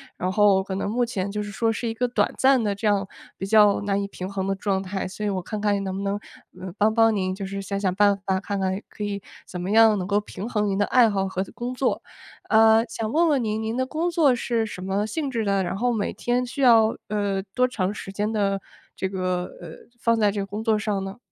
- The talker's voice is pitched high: Yes, high, 205 Hz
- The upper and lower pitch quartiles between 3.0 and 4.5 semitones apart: No, narrow, 2.6 semitones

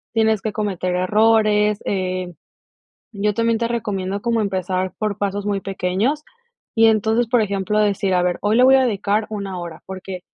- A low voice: No, high, 205 Hz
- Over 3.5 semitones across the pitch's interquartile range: No, average, 2.8 semitones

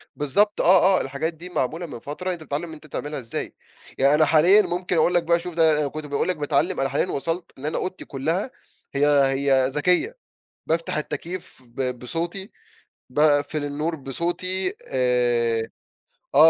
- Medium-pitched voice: Yes, medium, 155 Hz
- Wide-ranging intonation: No, average, 4.1 semitones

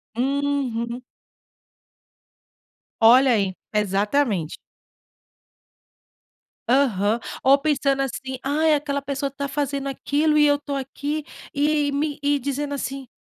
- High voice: Yes, very high, 275 Hz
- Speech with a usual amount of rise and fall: No, narrow, 2.3 semitones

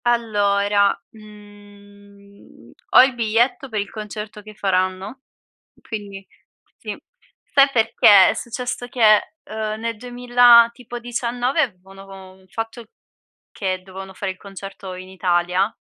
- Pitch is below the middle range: No, high, 210 Hz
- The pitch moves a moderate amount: Yes, average, 3.2 semitones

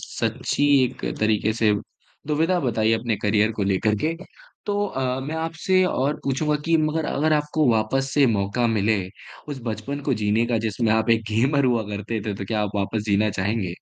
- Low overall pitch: Yes, low, 115 Hz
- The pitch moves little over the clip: No, average, 5.1 semitones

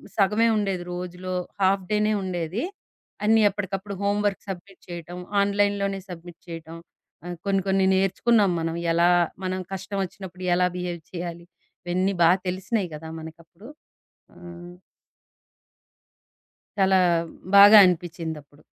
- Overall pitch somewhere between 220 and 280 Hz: No, medium, 185 Hz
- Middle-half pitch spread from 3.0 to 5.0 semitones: No, narrow, 2.4 semitones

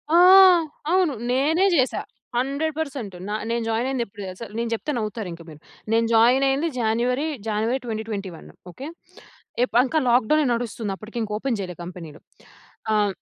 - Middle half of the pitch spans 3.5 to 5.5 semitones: Yes, average, 4.2 semitones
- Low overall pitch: No, high, 235 Hz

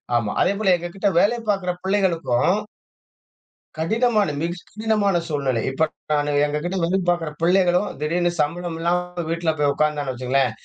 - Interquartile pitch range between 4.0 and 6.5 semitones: Yes, average, 4.3 semitones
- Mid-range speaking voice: Yes, medium, 175 Hz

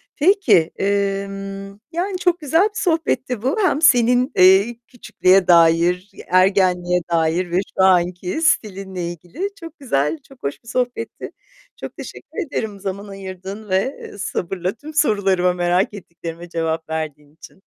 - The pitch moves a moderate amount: No, wide, 5.9 semitones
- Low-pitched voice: No, high, 195 Hz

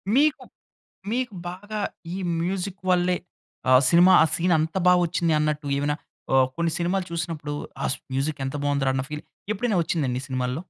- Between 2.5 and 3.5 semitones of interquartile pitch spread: No, average, 4.1 semitones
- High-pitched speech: No, medium, 170 Hz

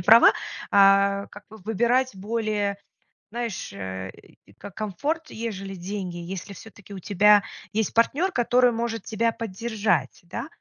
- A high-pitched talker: Yes, high, 210 Hz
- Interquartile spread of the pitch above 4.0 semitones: No, average, 3.1 semitones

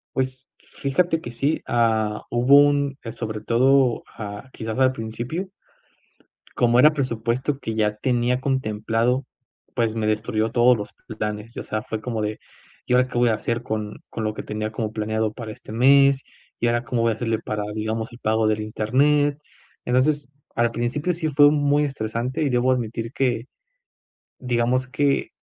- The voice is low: Yes, low, 120 Hz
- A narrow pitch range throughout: No, average, 3.2 semitones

